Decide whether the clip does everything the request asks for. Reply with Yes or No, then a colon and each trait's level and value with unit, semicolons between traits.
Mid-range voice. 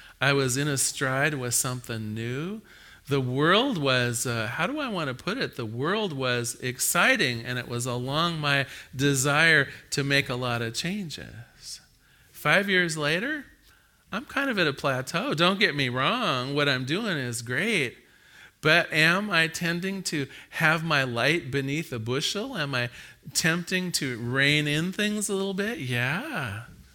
Yes: medium, 145 Hz